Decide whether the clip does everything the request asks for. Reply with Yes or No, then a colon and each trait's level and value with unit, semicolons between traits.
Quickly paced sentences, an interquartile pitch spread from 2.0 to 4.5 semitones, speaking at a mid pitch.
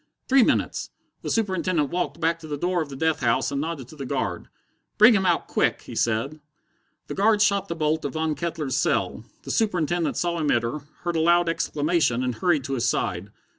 Yes: fast, 210 wpm; average, 4.0 semitones; medium, 160 Hz